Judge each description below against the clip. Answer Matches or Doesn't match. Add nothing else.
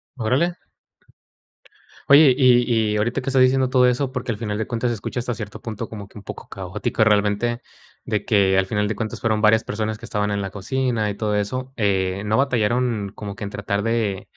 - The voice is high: Doesn't match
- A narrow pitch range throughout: Doesn't match